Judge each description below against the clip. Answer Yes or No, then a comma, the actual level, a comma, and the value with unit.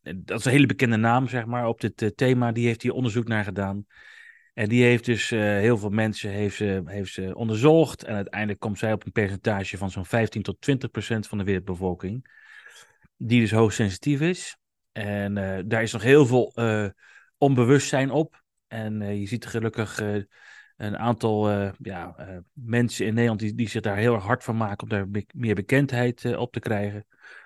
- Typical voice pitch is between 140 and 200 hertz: No, low, 110 Hz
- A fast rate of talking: Yes, fast, 205 wpm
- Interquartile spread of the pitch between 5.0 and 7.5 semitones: No, average, 2.9 semitones